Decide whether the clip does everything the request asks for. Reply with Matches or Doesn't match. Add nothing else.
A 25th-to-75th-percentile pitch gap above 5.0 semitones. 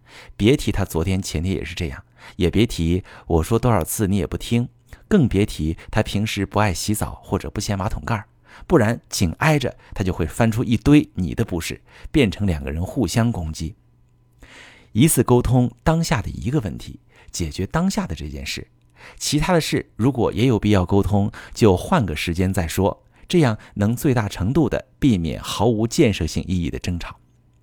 Matches